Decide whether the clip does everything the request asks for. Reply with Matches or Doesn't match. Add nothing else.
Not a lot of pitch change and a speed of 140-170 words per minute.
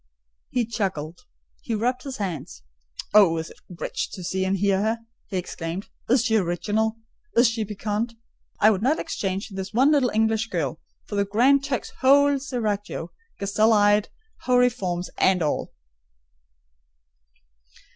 Doesn't match